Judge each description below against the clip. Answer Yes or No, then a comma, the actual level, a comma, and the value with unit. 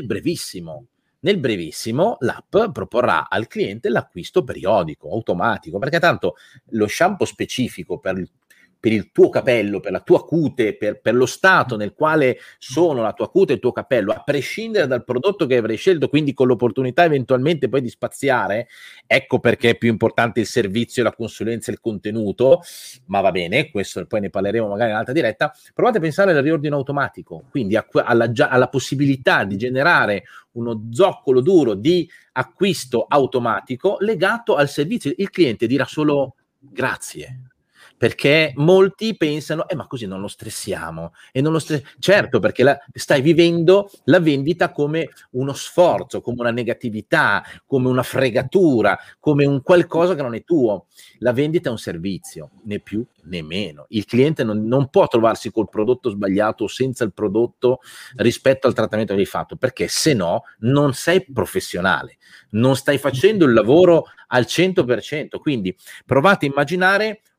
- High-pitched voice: No, low, 135 Hz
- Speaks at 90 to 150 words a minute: No, average, 165 wpm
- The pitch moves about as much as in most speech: No, wide, 6.2 semitones